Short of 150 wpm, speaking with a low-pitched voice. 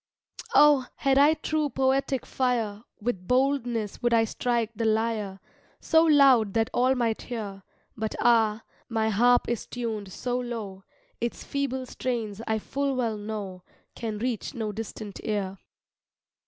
No: average, 140 wpm; high, 230 Hz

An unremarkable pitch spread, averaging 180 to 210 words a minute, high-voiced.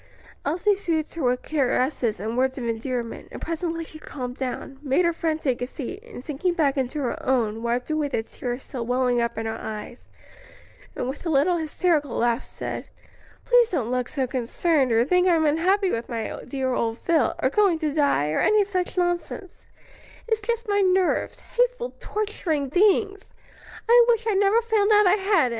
No: wide, 7.1 semitones; average, 190 wpm; very high, 305 Hz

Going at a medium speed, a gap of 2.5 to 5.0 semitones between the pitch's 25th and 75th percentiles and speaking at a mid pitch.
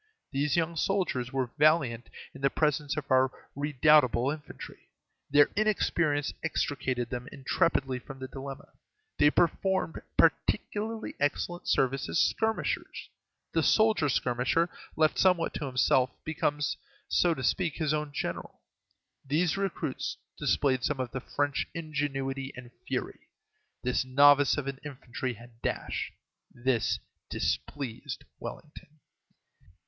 No: slow, 125 wpm; average, 3.1 semitones; medium, 145 Hz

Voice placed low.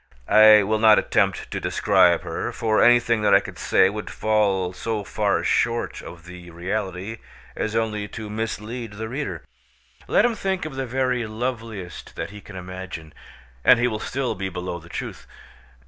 Yes: low, 110 Hz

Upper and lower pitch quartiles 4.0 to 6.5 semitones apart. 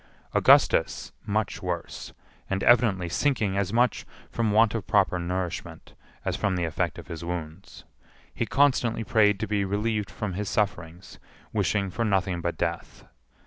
No: average, 3.5 semitones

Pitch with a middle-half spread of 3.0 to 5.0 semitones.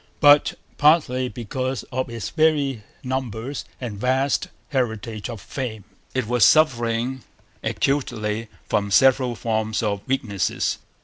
Yes: average, 3.3 semitones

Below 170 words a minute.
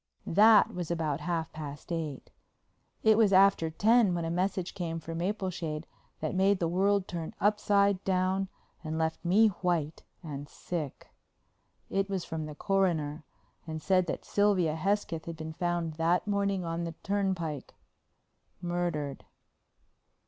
Yes: average, 140 wpm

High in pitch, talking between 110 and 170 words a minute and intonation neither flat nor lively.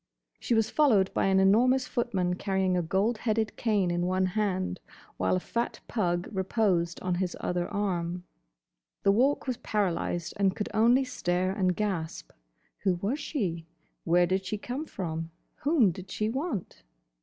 Yes: high, 195 Hz; average, 160 wpm; average, 3.9 semitones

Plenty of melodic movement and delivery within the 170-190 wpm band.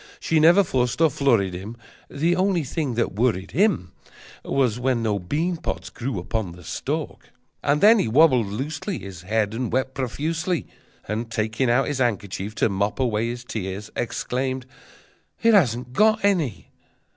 No: wide, 6.2 semitones; average, 160 wpm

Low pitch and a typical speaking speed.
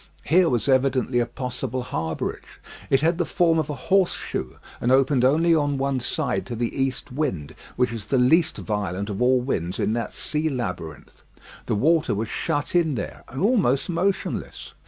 Yes: low, 130 Hz; average, 180 wpm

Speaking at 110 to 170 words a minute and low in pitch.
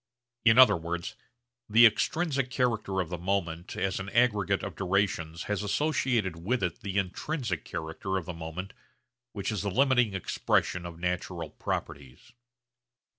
Yes: average, 145 wpm; very low, 95 Hz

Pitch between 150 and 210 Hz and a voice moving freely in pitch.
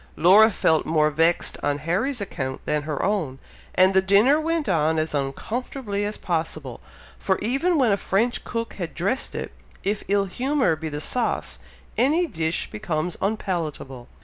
Yes: high, 190 Hz; wide, 6.4 semitones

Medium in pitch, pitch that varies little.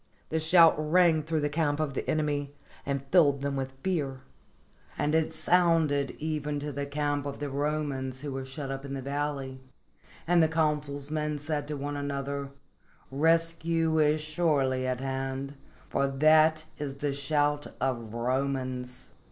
Yes: medium, 145 Hz; narrow, 2.2 semitones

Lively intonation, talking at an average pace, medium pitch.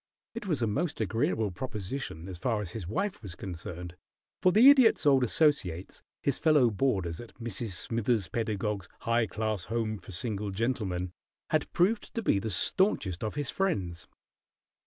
No: wide, 6.3 semitones; average, 160 wpm; low, 110 Hz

